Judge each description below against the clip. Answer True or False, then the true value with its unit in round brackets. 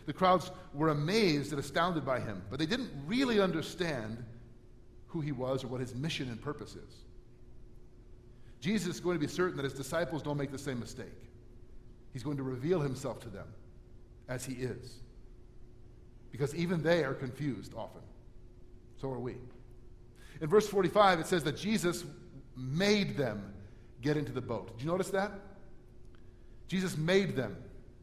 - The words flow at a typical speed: True (165 wpm)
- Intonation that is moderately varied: False (5.7 semitones)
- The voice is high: False (135 Hz)